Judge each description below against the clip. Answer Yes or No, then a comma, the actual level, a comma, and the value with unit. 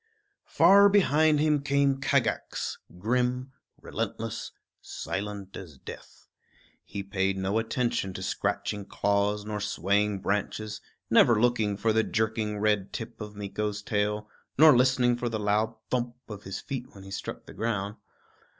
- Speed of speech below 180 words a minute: Yes, average, 140 wpm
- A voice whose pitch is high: No, low, 105 Hz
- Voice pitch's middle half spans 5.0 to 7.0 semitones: No, average, 3.2 semitones